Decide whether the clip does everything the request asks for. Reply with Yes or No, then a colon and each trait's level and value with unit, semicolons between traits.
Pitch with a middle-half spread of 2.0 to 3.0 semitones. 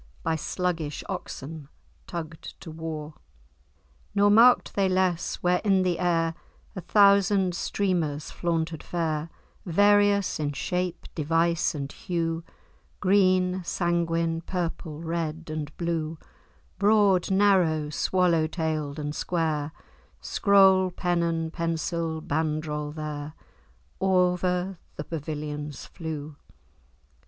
Yes: average, 2.7 semitones